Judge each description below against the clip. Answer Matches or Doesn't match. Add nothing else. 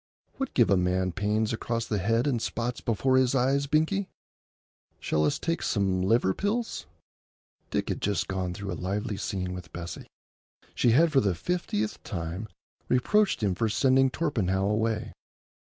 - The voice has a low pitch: Matches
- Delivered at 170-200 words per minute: Doesn't match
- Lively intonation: Matches